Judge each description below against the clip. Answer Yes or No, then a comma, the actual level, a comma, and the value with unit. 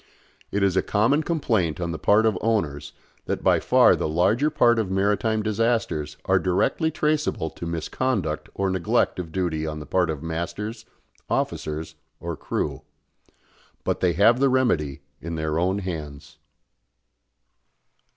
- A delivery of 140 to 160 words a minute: Yes, average, 150 wpm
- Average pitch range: No, wide, 5.7 semitones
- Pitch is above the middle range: No, very low, 95 Hz